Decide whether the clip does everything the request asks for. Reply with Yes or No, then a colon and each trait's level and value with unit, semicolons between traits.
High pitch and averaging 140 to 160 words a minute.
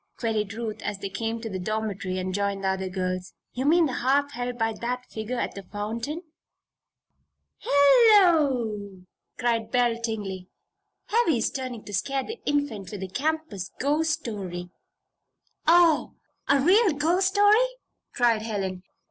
Yes: high, 235 Hz; average, 145 wpm